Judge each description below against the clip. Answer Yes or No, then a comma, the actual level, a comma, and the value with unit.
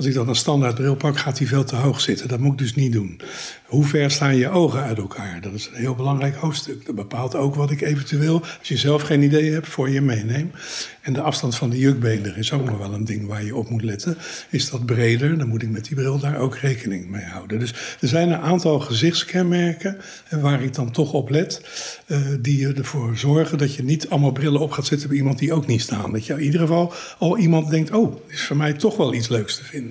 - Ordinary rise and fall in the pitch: Yes, average, 3.8 semitones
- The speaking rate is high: Yes, fast, 255 wpm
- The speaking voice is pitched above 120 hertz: Yes, medium, 140 Hz